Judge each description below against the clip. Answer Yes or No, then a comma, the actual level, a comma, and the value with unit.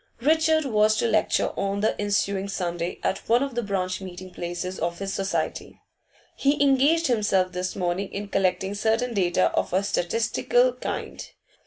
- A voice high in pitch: Yes, high, 200 Hz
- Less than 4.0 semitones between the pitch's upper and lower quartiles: No, average, 4.3 semitones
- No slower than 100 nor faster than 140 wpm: No, average, 160 wpm